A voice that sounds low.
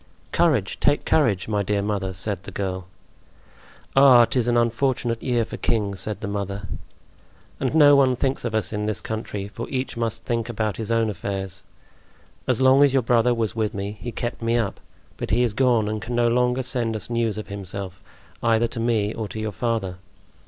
Yes: low, 115 Hz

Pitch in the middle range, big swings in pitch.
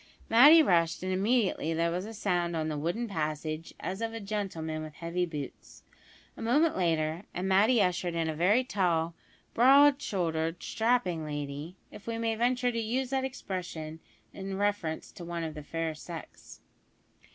Yes: medium, 180 Hz; wide, 5.7 semitones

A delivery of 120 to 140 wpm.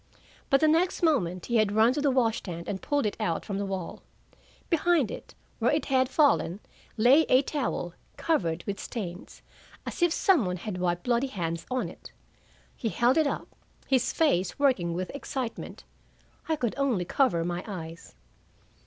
No: average, 175 wpm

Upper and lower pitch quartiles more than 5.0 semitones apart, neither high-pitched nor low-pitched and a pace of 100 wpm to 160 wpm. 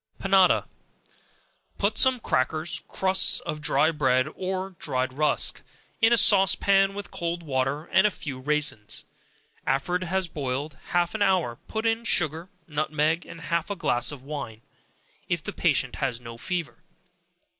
Yes: wide, 5.5 semitones; medium, 160 Hz; average, 155 wpm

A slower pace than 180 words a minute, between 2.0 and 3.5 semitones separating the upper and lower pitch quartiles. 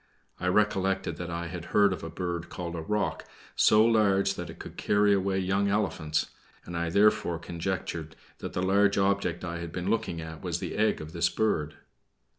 No: average, 195 wpm; average, 3.0 semitones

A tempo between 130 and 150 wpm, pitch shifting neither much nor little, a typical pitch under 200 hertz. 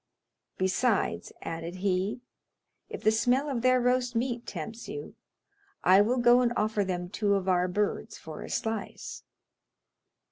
No: average, 145 wpm; average, 4.7 semitones; high, 215 Hz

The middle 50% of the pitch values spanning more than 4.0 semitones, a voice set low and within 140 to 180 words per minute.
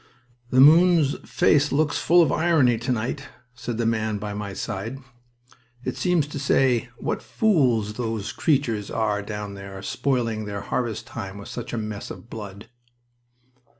Yes: average, 5.0 semitones; low, 115 Hz; average, 155 wpm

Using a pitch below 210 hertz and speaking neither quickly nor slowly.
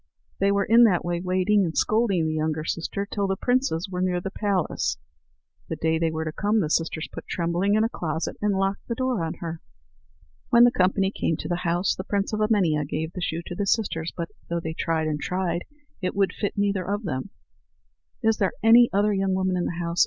No: medium, 185 Hz; fast, 220 wpm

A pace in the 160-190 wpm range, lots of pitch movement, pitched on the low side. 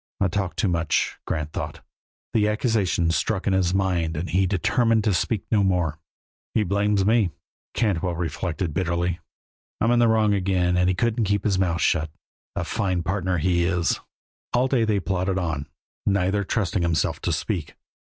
No: average, 170 wpm; average, 3.1 semitones; very low, 95 Hz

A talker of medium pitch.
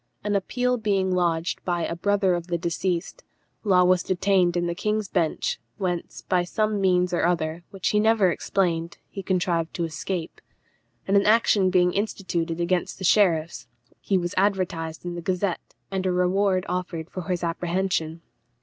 Yes: medium, 180 Hz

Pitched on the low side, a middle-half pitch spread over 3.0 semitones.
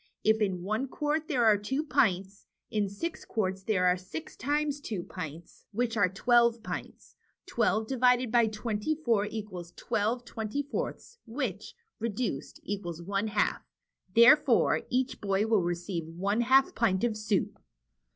No: high, 215 Hz; average, 4.2 semitones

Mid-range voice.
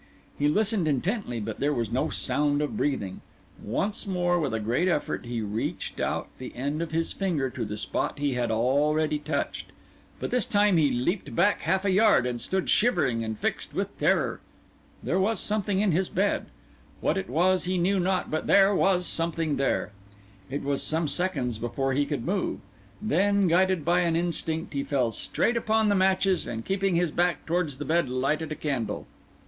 Yes: medium, 160 Hz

